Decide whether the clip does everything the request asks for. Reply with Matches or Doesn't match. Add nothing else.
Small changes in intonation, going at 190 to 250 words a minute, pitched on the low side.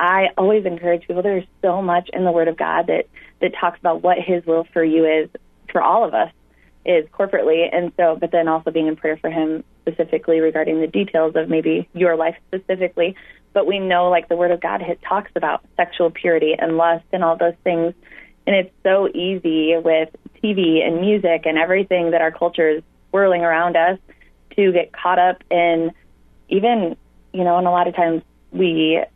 Doesn't match